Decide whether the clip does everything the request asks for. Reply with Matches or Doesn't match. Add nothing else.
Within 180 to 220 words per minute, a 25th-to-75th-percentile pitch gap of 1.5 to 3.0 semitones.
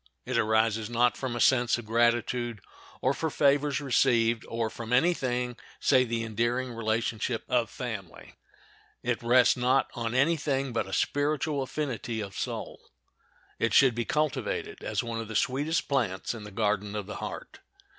Doesn't match